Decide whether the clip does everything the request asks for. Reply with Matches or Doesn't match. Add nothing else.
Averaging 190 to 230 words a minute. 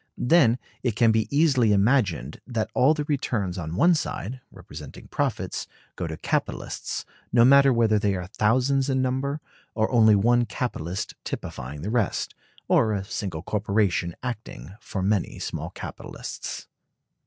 Doesn't match